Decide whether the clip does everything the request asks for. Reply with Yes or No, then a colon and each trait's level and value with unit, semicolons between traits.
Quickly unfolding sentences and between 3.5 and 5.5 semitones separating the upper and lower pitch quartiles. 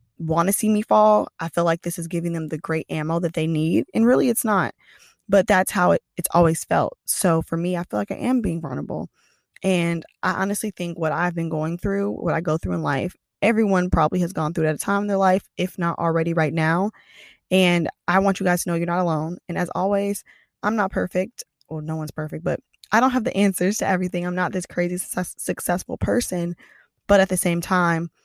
No: fast, 240 wpm; average, 3.0 semitones